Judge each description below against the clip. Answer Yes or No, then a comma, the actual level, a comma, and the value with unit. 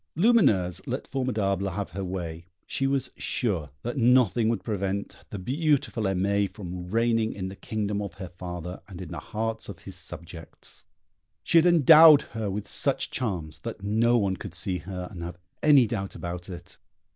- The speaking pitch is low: Yes, low, 100 Hz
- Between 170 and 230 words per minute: Yes, average, 175 wpm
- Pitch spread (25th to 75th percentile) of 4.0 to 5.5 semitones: Yes, average, 4.5 semitones